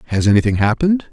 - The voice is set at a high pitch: No, low, 125 Hz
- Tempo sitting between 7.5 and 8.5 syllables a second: Yes, 8.1 syllables/s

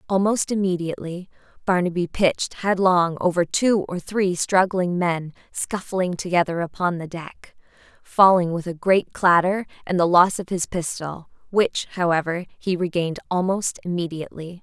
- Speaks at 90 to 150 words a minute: Yes, slow, 135 wpm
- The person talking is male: No, female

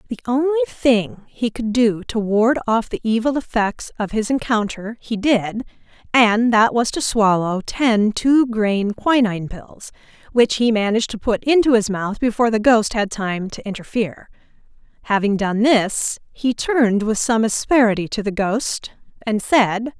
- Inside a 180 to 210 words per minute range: No, average, 165 wpm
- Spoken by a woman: Yes, female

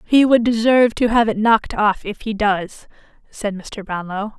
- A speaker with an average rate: Yes, average, 190 wpm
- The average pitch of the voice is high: Yes, high, 215 Hz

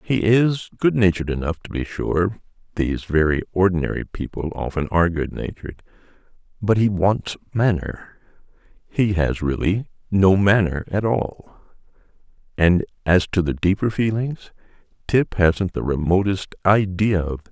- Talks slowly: Yes, slow, 125 wpm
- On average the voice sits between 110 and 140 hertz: No, very low, 95 Hz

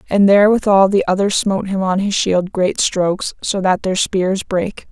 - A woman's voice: Yes, female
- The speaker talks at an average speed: Yes, average, 195 wpm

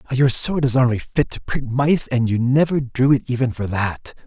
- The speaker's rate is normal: No, fast, 225 wpm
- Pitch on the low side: Yes, low, 125 Hz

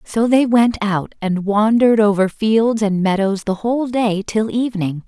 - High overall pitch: Yes, high, 215 Hz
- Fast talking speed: No, average, 175 wpm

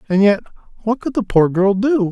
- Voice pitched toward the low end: No, high, 205 Hz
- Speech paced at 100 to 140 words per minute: No, fast, 225 wpm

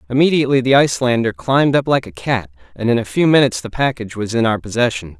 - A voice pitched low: Yes, low, 120 Hz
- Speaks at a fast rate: Yes, fast, 220 wpm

